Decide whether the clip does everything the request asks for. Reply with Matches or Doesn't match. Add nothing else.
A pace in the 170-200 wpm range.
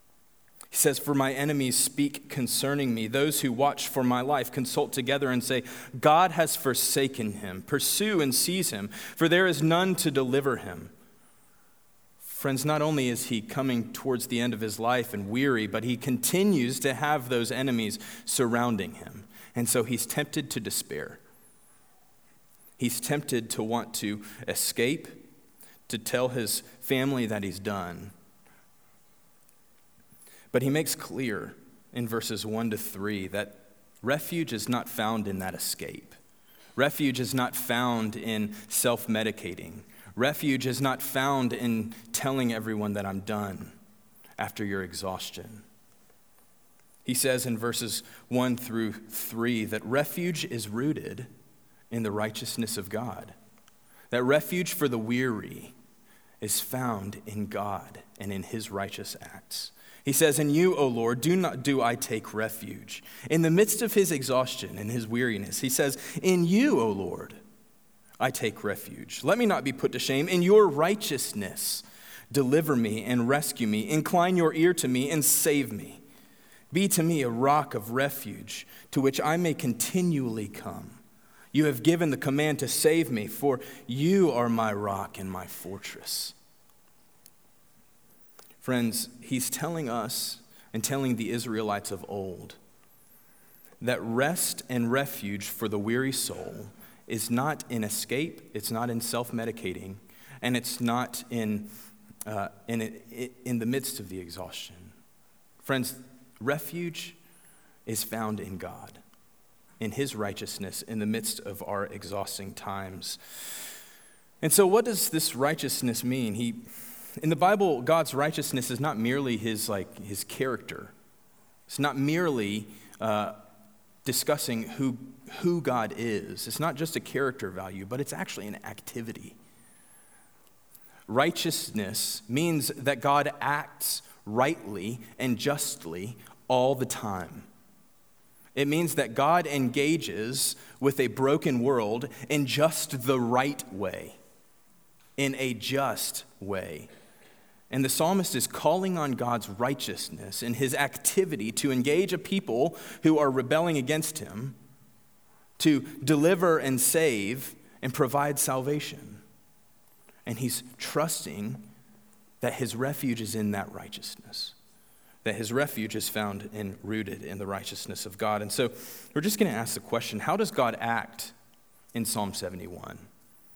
Doesn't match